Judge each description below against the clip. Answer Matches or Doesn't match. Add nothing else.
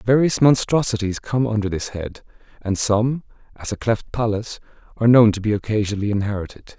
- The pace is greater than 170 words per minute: Doesn't match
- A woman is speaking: Doesn't match